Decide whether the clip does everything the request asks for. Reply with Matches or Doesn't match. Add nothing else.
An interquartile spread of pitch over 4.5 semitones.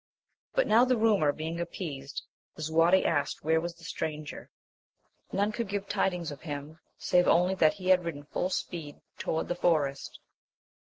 Doesn't match